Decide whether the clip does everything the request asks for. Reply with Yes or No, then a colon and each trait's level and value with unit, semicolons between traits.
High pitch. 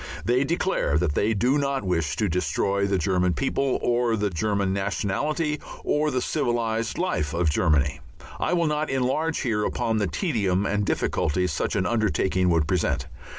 No: low, 105 Hz